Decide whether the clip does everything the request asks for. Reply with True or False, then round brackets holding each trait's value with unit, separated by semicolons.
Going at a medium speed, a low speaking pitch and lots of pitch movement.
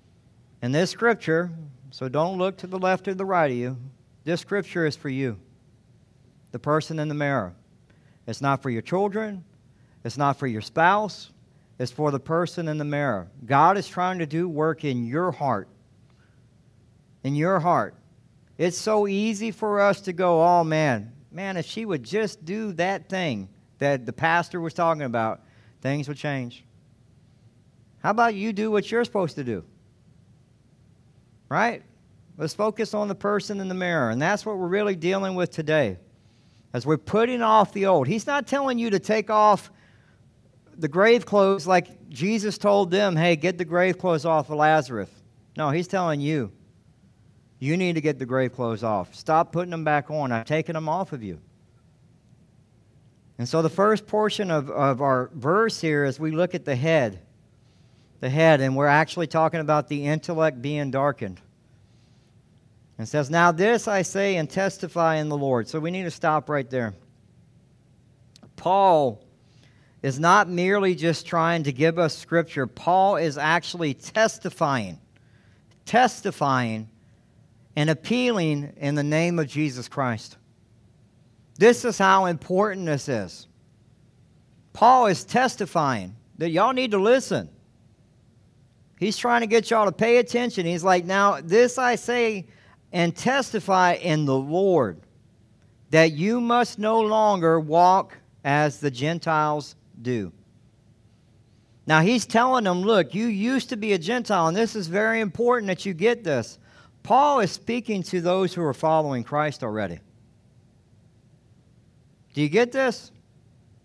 False (160 wpm; 160 Hz; 6.9 semitones)